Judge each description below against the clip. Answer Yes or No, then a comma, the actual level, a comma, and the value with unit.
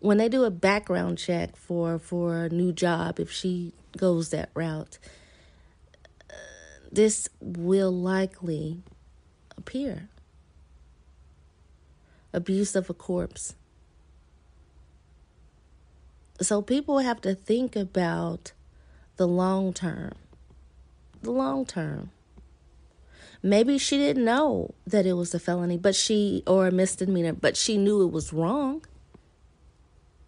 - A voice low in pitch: No, medium, 165 Hz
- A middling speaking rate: No, slow, 115 wpm